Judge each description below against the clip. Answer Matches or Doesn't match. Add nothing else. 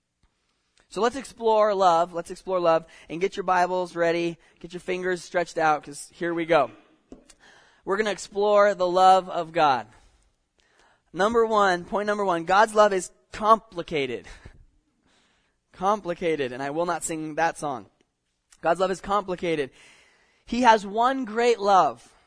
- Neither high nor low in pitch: Matches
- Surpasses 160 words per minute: Doesn't match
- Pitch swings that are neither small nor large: Matches